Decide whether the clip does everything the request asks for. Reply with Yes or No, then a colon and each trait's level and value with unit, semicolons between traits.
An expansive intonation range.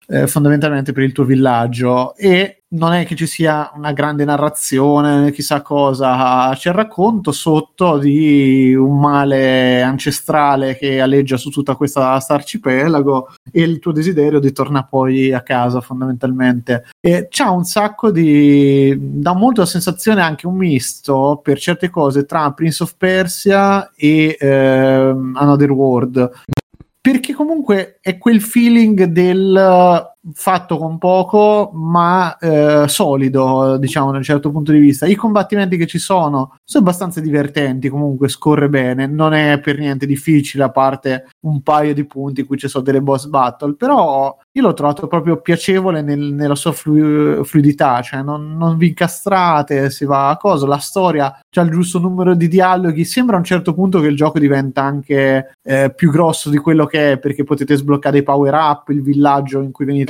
No: average, 4.0 semitones